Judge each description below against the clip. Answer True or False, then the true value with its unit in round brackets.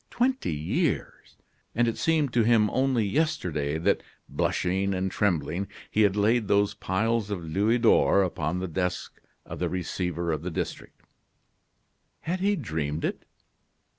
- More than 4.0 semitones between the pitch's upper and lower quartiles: True (5.2 semitones)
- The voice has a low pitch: True (100 Hz)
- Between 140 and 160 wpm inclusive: True (145 wpm)